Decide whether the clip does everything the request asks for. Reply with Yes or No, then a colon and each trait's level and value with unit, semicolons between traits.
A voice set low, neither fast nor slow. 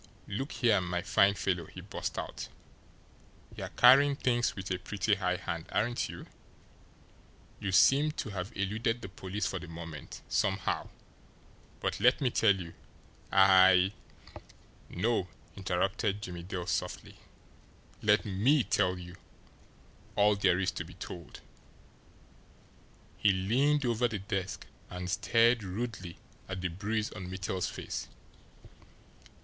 No: low, 100 Hz; slow, 130 wpm